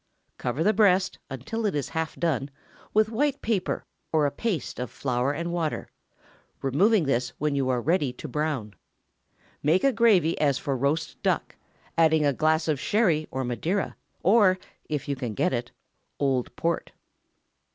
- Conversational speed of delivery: Yes, average, 160 wpm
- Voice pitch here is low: No, medium, 155 Hz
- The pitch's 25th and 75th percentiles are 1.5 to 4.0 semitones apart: No, wide, 5.6 semitones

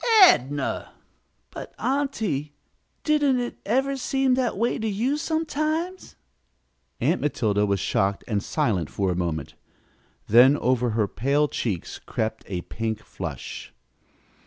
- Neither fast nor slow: No, slow, 125 wpm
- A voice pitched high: No, medium, 145 Hz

